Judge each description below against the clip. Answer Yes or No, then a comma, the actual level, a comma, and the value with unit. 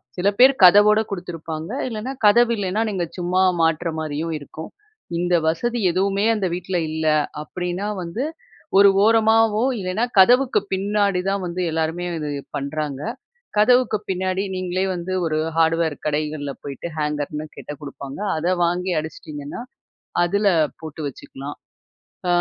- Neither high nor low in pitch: Yes, medium, 180 Hz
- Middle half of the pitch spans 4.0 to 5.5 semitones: Yes, average, 4.3 semitones